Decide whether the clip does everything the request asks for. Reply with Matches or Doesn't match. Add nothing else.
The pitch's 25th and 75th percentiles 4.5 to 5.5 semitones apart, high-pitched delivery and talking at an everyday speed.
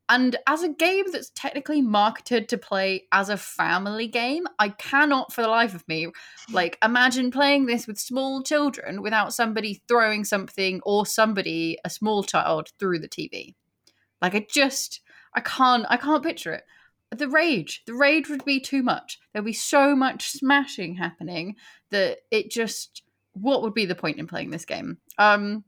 Matches